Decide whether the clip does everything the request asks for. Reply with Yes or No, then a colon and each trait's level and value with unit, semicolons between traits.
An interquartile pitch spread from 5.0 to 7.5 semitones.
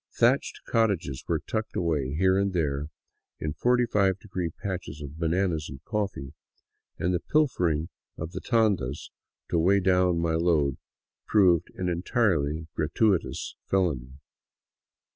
No: average, 4.1 semitones